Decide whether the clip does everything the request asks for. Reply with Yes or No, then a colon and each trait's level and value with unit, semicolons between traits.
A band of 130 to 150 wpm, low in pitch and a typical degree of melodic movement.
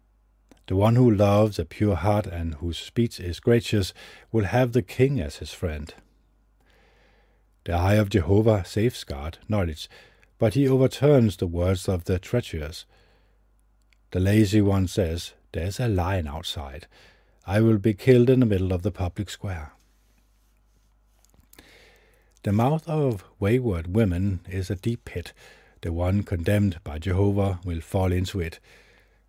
Yes: average, 145 wpm; low, 100 Hz; average, 3.5 semitones